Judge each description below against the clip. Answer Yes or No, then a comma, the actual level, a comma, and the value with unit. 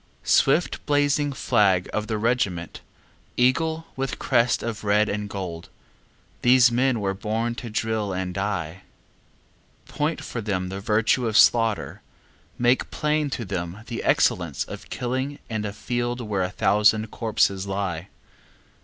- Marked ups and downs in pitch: No, average, 4.0 semitones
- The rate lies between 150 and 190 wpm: No, average, 140 wpm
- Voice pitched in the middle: No, low, 110 Hz